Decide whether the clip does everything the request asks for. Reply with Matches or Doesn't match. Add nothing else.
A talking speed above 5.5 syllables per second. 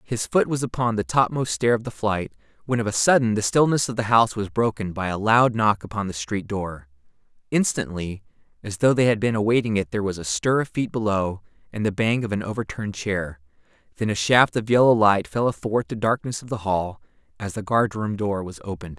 Matches